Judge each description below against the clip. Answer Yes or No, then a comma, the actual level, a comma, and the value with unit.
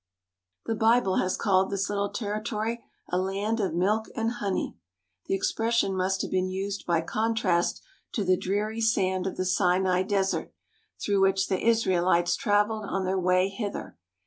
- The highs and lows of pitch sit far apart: No, narrow, 2.5 semitones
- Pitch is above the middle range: Yes, high, 195 Hz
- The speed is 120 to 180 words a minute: Yes, average, 160 wpm